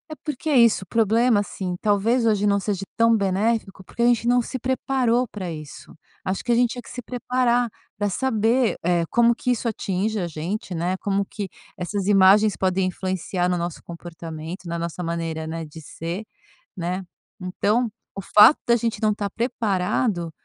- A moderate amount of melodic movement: Yes, average, 4.5 semitones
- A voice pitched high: Yes, high, 205 Hz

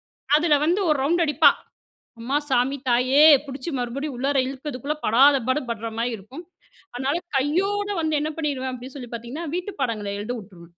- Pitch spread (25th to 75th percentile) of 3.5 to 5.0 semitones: Yes, average, 3.8 semitones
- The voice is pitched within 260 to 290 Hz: Yes, very high, 270 Hz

